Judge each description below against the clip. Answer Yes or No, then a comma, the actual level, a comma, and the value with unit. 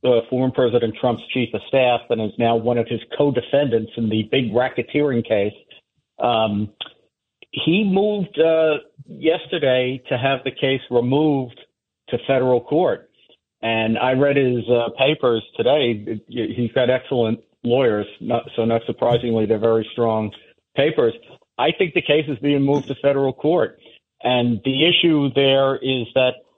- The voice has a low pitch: Yes, low, 125 Hz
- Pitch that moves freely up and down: No, average, 3.4 semitones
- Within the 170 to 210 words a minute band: No, average, 150 wpm